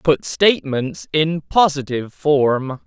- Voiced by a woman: No, male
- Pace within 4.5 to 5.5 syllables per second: No, 3.6 syllables/s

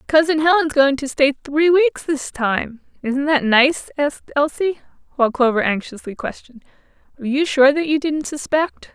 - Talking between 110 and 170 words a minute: Yes, average, 160 wpm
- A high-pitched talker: Yes, very high, 285 Hz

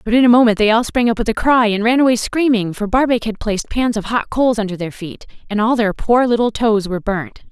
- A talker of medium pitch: No, high, 225 Hz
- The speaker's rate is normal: No, fast, 270 wpm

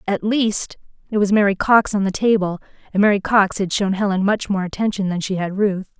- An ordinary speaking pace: No, fast, 220 wpm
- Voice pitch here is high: Yes, high, 200 Hz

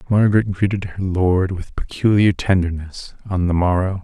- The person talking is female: No, male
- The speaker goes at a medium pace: Yes, average, 150 wpm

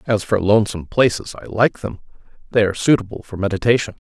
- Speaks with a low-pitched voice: Yes, low, 105 Hz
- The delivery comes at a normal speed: Yes, average, 175 wpm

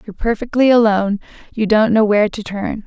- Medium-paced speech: Yes, average, 190 wpm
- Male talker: No, female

